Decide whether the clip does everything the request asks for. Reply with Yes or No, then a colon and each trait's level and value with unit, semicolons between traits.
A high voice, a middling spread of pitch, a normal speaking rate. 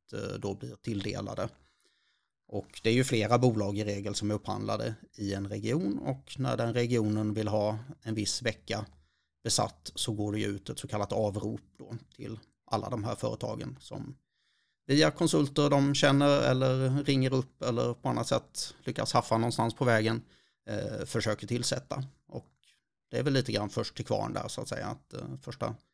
No: low, 115 Hz; average, 3.9 semitones; average, 180 wpm